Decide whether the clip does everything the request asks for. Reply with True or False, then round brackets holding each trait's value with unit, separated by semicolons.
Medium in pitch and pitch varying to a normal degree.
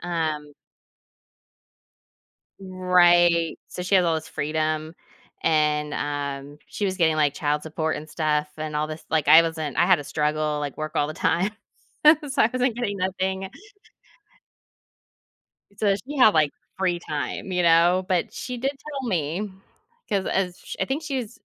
True (170 Hz; 3.9 semitones)